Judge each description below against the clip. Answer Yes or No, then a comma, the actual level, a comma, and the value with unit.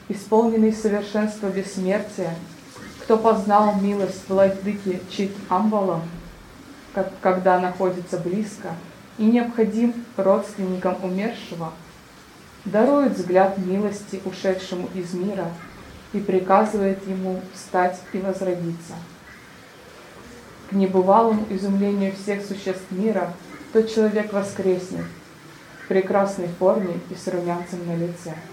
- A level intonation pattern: Yes, narrow, 2.0 semitones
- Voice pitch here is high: Yes, high, 195 Hz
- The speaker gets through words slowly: Yes, slow, 95 wpm